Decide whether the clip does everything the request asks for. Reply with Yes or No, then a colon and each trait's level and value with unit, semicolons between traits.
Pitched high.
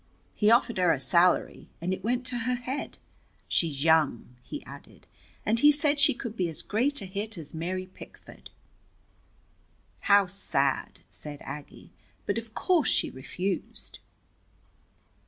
Yes: high, 195 Hz